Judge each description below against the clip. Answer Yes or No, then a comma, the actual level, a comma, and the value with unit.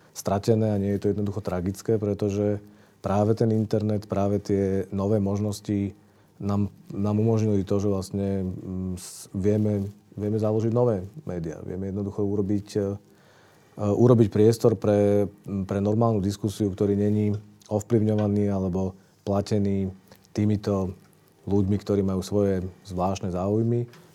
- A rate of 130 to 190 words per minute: No, average, 115 wpm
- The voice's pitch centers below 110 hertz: Yes, low, 100 Hz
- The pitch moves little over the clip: Yes, narrow, 1.2 semitones